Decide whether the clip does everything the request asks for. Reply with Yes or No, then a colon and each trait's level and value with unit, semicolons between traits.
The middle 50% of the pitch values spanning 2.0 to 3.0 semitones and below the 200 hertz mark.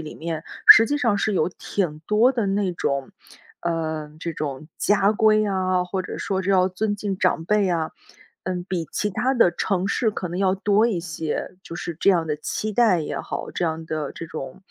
No: average, 4.0 semitones; medium, 185 Hz